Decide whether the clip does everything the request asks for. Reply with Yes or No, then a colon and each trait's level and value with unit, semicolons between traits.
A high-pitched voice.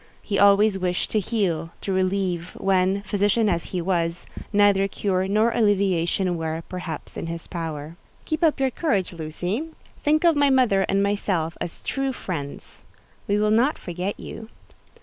Yes: high, 195 Hz